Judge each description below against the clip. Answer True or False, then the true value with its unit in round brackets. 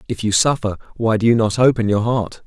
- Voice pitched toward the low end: True (110 Hz)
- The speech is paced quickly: True (245 wpm)